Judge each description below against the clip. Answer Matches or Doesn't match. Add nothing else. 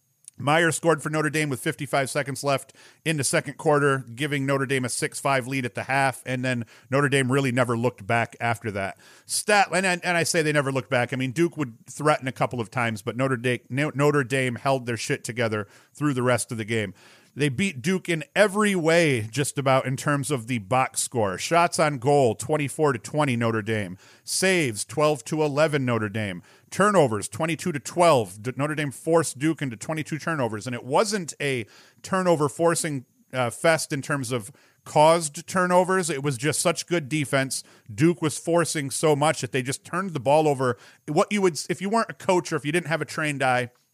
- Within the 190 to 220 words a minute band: Matches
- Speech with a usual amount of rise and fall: Matches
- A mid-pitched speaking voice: Matches